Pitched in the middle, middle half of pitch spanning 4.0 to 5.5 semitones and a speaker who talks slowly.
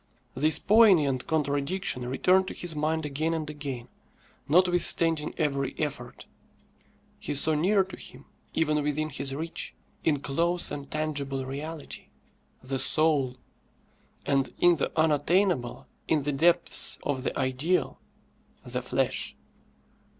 No: medium, 150 Hz; average, 3.1 semitones; slow, 120 wpm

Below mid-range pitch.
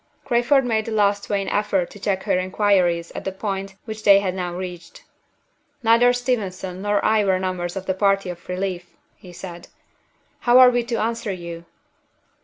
No: high, 195 Hz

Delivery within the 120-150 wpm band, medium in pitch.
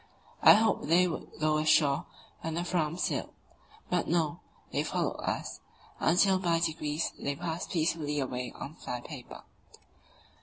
Yes: average, 145 wpm; medium, 160 Hz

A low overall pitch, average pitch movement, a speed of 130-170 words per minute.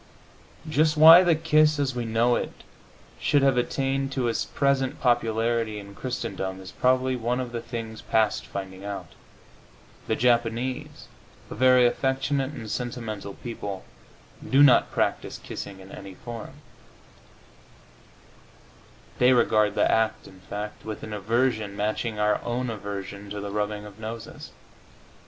Yes: low, 115 Hz; average, 3.7 semitones; average, 140 wpm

